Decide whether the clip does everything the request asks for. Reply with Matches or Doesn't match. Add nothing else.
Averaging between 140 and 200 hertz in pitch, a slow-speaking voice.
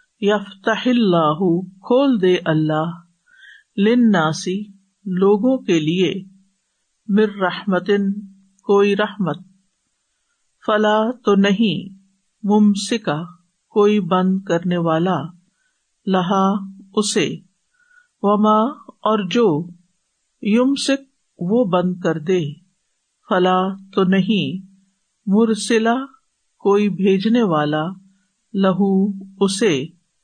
Matches